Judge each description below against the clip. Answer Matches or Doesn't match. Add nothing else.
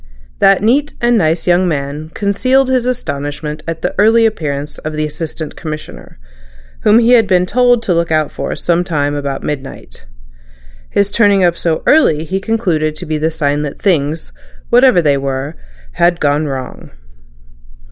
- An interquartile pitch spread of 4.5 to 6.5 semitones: Matches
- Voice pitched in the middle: Matches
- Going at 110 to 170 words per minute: Matches